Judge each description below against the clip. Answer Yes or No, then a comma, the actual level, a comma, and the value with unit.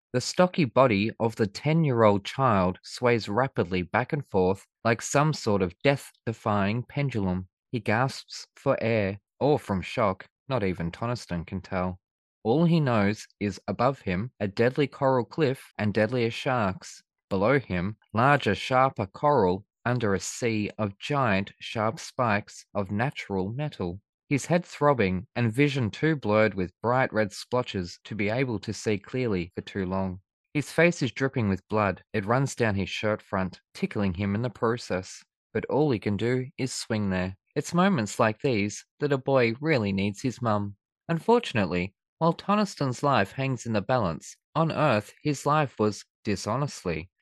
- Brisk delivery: No, average, 165 wpm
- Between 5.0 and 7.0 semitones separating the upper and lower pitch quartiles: Yes, wide, 5.4 semitones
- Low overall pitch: Yes, low, 115 Hz